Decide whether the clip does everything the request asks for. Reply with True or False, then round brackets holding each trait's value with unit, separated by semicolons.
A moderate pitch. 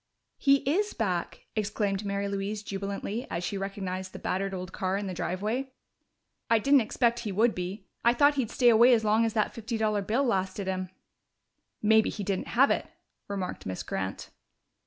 False (205 Hz)